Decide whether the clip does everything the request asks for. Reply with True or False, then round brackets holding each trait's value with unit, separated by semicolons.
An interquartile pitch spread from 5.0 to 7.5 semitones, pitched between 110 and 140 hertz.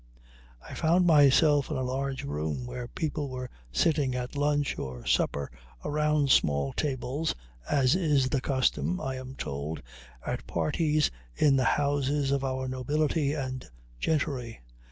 False (2.8 semitones; 135 Hz)